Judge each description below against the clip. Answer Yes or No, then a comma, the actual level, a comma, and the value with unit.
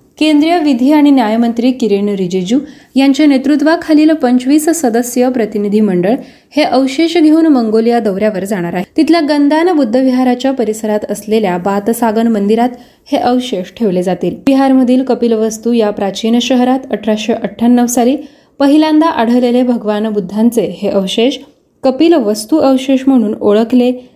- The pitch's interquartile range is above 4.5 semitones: No, average, 4.1 semitones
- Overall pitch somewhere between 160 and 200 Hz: No, high, 245 Hz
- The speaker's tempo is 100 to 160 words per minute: Yes, average, 125 wpm